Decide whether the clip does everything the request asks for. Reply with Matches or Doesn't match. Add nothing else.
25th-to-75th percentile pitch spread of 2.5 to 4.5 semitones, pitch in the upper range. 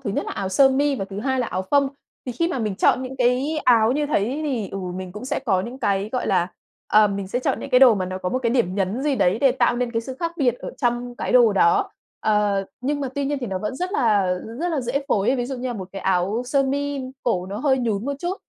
Doesn't match